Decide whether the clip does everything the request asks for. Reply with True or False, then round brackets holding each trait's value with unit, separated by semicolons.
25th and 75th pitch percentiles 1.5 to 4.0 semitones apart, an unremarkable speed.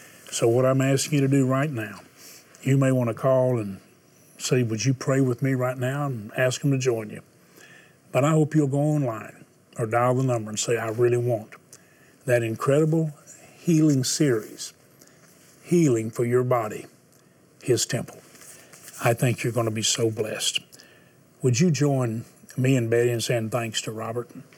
True (2.8 semitones; 180 wpm)